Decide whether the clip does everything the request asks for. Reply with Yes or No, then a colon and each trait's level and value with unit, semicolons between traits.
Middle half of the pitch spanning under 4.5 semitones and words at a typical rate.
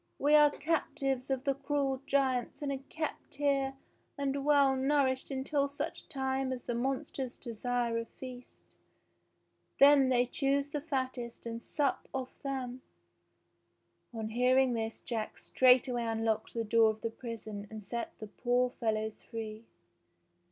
Yes: average, 2.9 semitones; average, 145 wpm